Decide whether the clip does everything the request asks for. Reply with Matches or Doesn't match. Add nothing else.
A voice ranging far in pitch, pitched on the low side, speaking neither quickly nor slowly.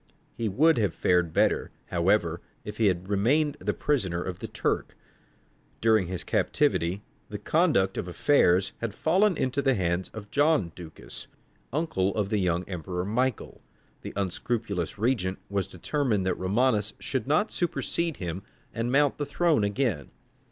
Matches